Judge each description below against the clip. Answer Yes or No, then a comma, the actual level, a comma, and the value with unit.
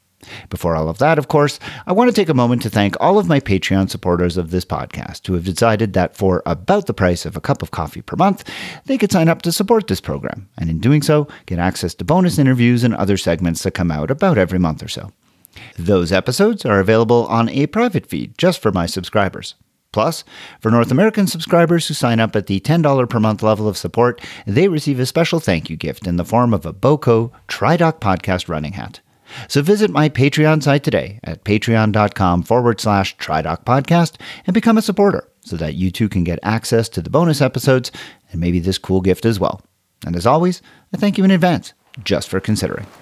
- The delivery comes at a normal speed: No, fast, 215 wpm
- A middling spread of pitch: No, wide, 8.4 semitones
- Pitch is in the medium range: No, low, 115 Hz